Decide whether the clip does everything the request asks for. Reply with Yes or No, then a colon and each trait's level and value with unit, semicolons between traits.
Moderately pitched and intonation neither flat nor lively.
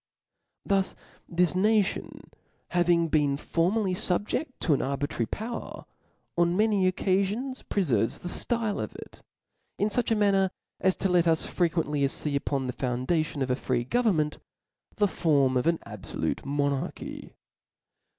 No: medium, 175 Hz; wide, 5.9 semitones